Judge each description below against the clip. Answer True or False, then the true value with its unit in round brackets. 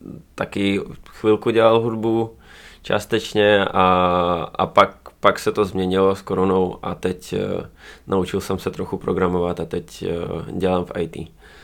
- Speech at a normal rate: True (135 wpm)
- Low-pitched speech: True (95 Hz)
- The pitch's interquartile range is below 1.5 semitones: False (2.2 semitones)